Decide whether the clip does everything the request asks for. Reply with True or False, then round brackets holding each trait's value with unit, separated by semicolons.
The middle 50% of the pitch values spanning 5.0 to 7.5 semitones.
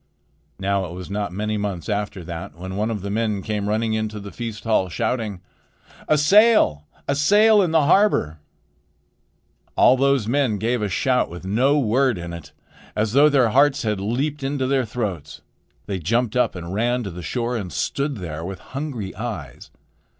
True (5.4 semitones)